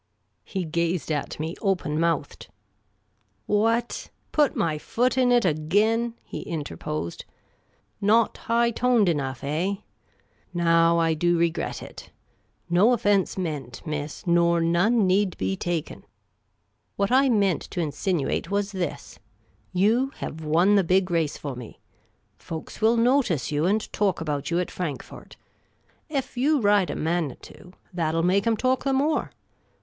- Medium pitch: Yes, medium, 180 Hz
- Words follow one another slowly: No, average, 150 wpm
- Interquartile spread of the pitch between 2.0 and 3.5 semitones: No, average, 5.3 semitones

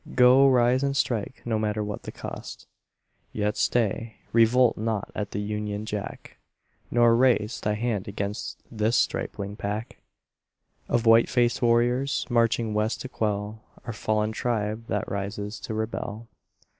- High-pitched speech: No, low, 110 Hz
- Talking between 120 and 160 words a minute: Yes, average, 145 wpm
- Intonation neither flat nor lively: No, narrow, 2.2 semitones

